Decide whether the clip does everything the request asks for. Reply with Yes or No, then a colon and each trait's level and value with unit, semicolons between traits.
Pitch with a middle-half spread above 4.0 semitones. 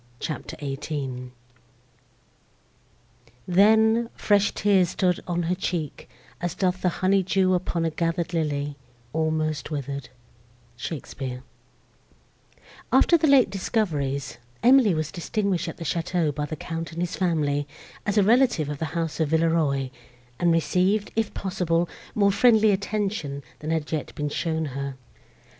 Yes: average, 4.5 semitones